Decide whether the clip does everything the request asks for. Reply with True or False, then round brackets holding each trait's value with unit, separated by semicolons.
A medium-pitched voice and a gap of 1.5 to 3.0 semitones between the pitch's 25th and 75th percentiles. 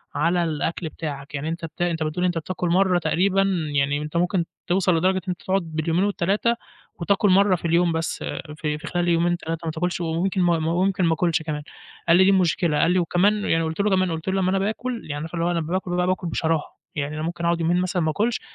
True (175 Hz; 2.4 semitones)